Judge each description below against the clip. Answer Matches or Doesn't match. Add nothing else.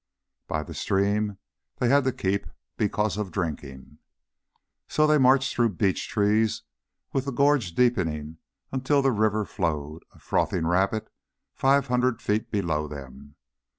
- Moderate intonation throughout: Doesn't match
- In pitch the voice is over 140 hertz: Doesn't match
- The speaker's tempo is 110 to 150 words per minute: Matches